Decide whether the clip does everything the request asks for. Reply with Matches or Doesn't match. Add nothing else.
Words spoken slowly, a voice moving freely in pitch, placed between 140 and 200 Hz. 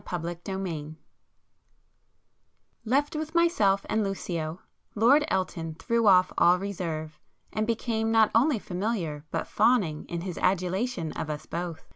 Doesn't match